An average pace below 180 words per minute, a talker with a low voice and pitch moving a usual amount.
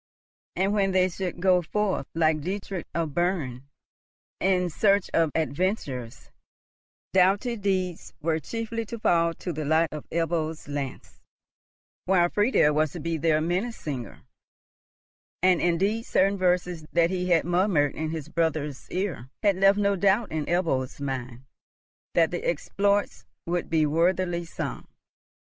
No: average, 140 wpm; medium, 175 Hz; average, 3.5 semitones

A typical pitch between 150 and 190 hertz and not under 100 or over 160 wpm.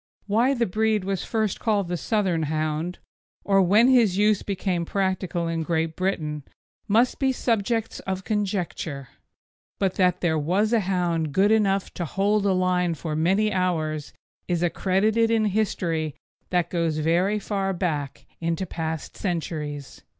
Yes: medium, 185 Hz; average, 150 wpm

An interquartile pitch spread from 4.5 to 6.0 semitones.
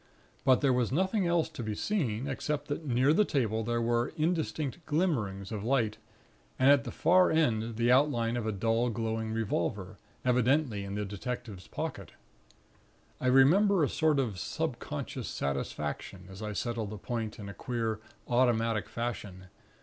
Yes: average, 4.8 semitones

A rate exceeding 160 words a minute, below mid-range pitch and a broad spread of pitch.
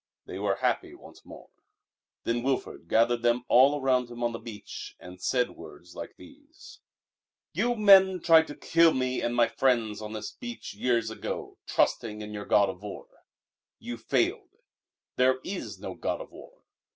Yes: average, 170 wpm; low, 120 Hz; wide, 6.8 semitones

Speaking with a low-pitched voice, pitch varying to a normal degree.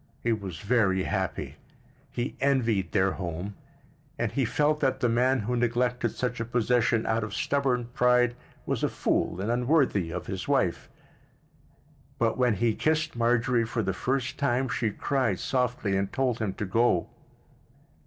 Yes: low, 120 Hz; average, 3.2 semitones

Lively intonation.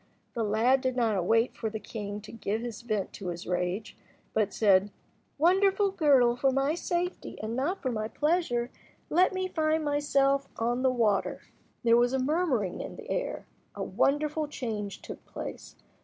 Yes: wide, 5.8 semitones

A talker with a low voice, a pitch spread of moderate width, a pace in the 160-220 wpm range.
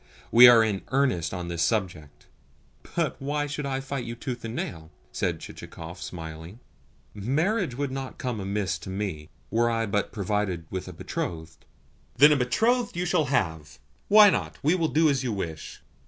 No: low, 115 Hz; wide, 7.8 semitones; average, 175 wpm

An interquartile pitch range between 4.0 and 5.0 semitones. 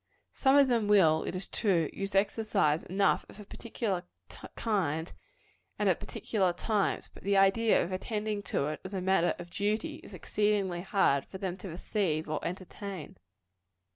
No: average, 3.1 semitones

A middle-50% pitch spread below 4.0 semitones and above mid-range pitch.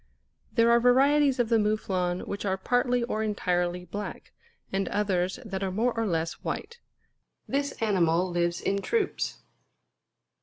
No: average, 5.1 semitones; high, 205 Hz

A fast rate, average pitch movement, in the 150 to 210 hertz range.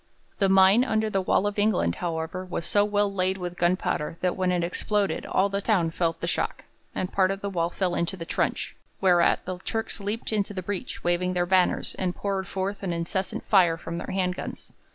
No: fast, 215 wpm; narrow, 2.3 semitones; medium, 185 Hz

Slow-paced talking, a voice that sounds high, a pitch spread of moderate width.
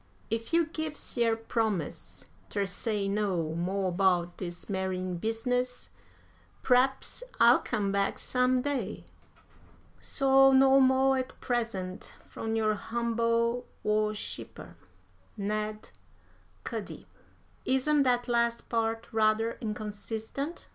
Yes: slow, 105 wpm; high, 225 Hz; average, 3.7 semitones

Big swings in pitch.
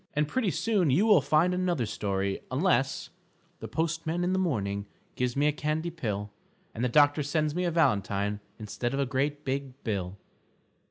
Yes: wide, 6.5 semitones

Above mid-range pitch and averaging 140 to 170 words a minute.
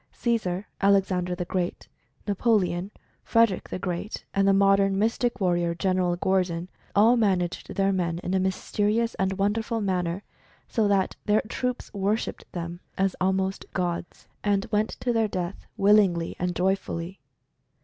Yes: high, 195 Hz; average, 145 wpm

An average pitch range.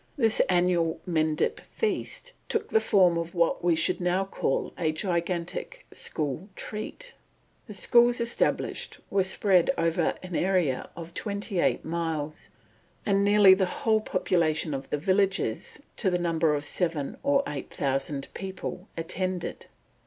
Yes: average, 3.5 semitones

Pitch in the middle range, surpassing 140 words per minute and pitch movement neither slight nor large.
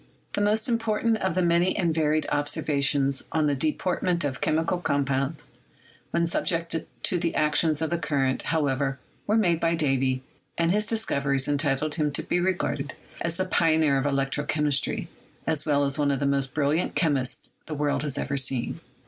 Yes: medium, 150 Hz; average, 175 wpm; average, 3.4 semitones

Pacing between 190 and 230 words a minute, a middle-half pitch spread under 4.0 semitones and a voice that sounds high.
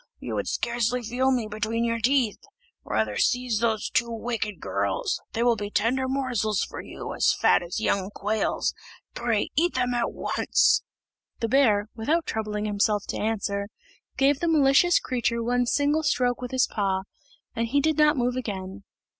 No: average, 170 wpm; average, 3.5 semitones; high, 235 Hz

